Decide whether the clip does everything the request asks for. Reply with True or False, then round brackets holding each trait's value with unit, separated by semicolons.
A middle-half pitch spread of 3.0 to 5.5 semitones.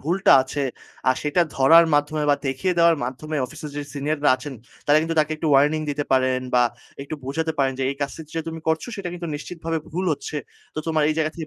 False (2.5 semitones)